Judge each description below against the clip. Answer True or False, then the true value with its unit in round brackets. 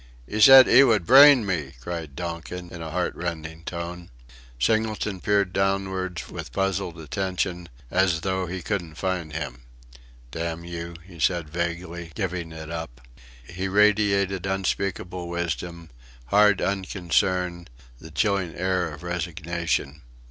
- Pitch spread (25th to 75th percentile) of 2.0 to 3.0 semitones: True (2.6 semitones)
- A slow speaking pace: True (125 wpm)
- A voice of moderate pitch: False (90 Hz)